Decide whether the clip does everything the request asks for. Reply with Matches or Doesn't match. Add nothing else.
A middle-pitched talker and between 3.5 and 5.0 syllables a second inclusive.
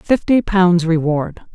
Matches